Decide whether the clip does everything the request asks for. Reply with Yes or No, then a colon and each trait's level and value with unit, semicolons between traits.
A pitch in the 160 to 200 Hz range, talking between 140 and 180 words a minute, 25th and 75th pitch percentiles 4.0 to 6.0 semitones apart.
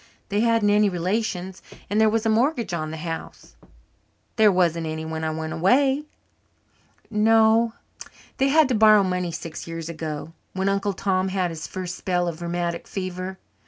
Yes: medium, 185 Hz; average, 165 wpm; average, 4.4 semitones